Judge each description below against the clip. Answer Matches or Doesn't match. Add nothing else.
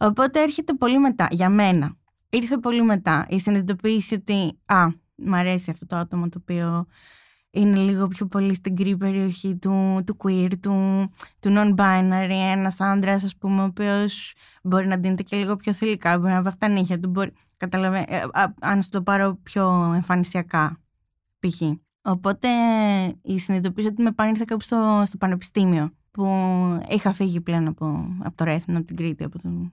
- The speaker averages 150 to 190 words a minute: Matches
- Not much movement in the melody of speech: Matches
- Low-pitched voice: Doesn't match